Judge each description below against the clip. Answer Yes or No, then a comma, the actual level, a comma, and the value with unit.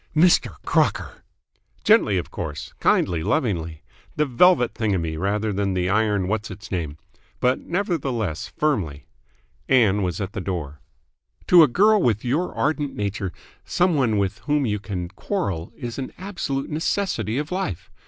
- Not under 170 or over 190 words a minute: No, average, 150 wpm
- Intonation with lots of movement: Yes, wide, 8.1 semitones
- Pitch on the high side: No, low, 110 Hz